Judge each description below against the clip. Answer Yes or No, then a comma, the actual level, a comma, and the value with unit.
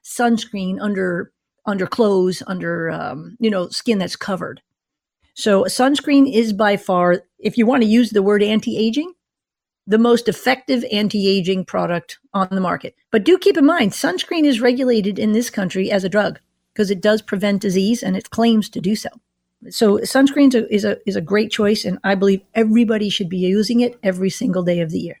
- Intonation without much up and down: No, average, 3.5 semitones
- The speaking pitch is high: Yes, high, 210 Hz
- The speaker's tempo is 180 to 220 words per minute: Yes, average, 200 wpm